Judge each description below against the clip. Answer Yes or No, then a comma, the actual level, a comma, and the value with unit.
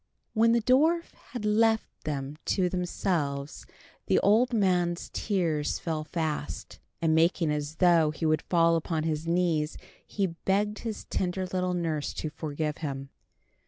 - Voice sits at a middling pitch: Yes, medium, 170 Hz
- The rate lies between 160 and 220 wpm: No, average, 145 wpm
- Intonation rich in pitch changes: No, average, 4.0 semitones